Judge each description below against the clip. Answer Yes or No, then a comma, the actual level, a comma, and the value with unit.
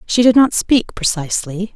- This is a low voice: No, high, 210 Hz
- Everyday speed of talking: Yes, average, 170 wpm